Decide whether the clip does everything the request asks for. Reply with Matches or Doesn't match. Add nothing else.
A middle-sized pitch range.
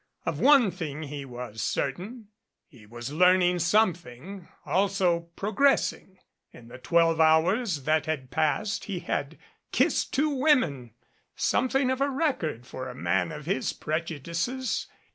Doesn't match